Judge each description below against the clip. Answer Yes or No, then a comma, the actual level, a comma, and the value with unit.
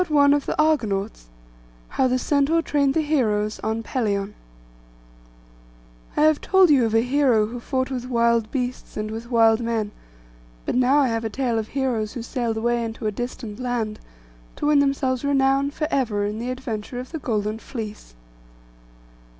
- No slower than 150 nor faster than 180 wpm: Yes, average, 175 wpm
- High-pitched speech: Yes, high, 245 Hz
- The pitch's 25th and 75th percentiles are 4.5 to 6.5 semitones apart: No, average, 3.7 semitones